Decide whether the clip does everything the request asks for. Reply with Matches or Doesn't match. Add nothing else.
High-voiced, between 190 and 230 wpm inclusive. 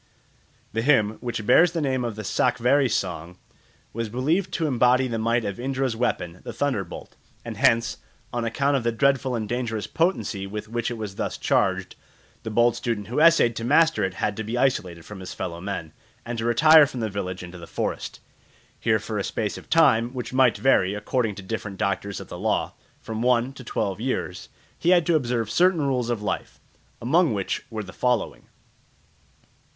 Doesn't match